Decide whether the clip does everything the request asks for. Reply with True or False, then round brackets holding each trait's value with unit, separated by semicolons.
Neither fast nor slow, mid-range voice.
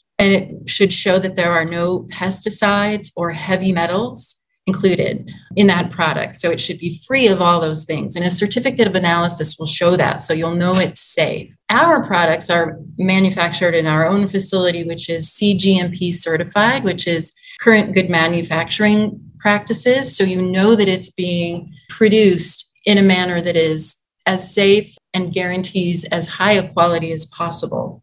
True (165 wpm; 180 Hz)